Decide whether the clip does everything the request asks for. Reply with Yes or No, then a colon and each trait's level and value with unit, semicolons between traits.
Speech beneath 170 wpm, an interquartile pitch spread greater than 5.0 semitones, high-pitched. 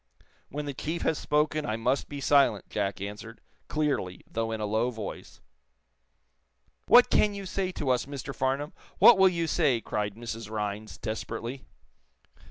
No: average, 160 wpm; wide, 5.4 semitones; low, 125 Hz